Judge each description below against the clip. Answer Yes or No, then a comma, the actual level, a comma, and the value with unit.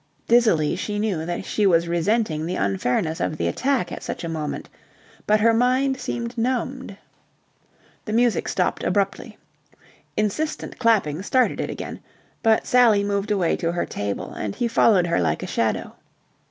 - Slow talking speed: No, average, 160 wpm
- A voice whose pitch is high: Yes, high, 205 Hz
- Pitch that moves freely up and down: Yes, wide, 5.8 semitones